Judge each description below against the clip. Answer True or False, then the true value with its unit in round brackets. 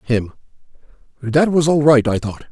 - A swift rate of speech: False (165 wpm)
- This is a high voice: False (135 Hz)